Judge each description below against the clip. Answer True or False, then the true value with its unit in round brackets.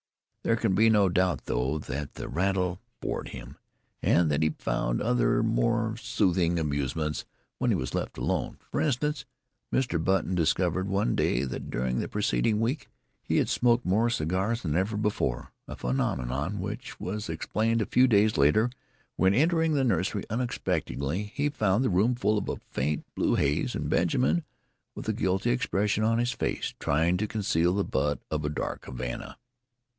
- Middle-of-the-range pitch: False (95 Hz)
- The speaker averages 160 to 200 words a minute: True (170 wpm)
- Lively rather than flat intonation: True (6.7 semitones)